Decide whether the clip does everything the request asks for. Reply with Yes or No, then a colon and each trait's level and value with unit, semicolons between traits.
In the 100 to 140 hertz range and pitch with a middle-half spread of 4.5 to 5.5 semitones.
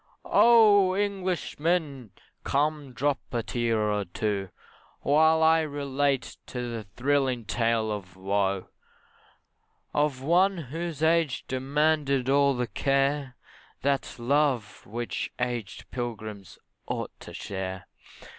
Yes: low, 135 Hz; average, 4.9 semitones